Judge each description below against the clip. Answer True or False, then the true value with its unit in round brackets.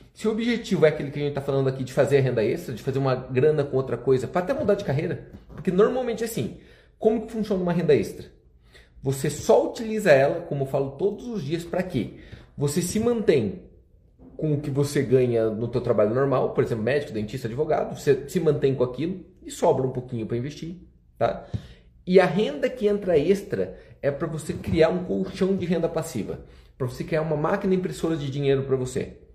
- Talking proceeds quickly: True (210 wpm)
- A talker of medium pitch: True (155 Hz)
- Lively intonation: True (6.2 semitones)